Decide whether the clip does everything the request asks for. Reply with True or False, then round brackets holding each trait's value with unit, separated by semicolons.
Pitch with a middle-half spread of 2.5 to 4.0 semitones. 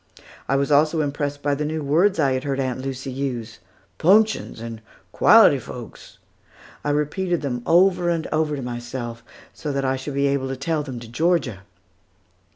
True (3.2 semitones)